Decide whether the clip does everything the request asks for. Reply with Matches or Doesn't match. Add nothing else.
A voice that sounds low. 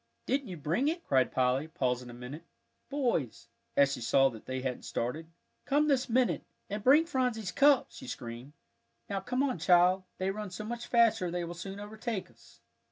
Doesn't match